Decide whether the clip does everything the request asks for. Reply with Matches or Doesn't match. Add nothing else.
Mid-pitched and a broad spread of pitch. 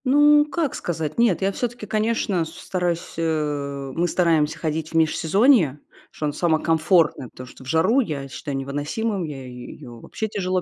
Matches